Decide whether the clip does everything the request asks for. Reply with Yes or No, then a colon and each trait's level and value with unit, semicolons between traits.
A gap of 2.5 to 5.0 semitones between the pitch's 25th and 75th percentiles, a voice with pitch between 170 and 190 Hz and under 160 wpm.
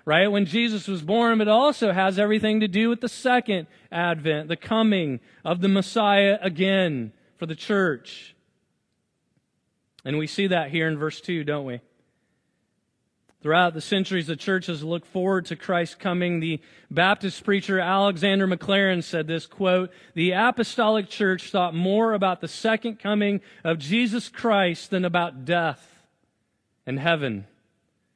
Yes: average, 3.7 semitones; medium, 185 Hz; average, 150 wpm